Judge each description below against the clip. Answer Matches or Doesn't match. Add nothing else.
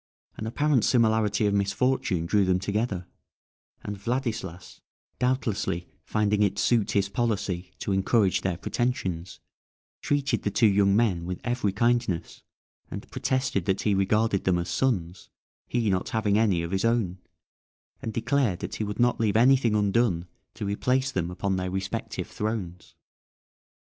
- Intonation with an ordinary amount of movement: Matches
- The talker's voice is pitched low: Matches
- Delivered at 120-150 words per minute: Matches